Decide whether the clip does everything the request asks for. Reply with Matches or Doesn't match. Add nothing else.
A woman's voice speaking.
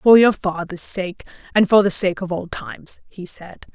Matches